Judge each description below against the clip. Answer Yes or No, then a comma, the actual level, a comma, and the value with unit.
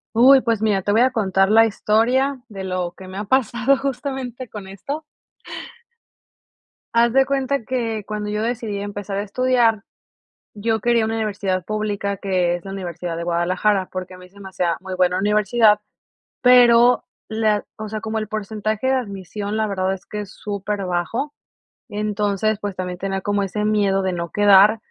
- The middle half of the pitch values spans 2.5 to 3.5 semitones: Yes, average, 2.9 semitones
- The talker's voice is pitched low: No, high, 210 Hz